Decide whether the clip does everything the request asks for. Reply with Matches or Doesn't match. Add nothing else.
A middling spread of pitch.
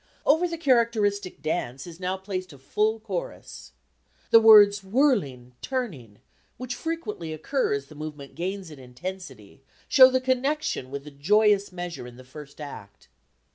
Doesn't match